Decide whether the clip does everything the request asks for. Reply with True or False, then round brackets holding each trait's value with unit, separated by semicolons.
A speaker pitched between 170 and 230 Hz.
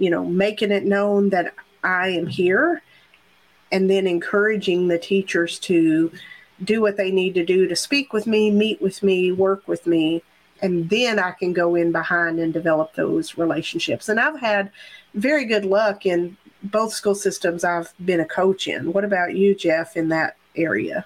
True (190 Hz)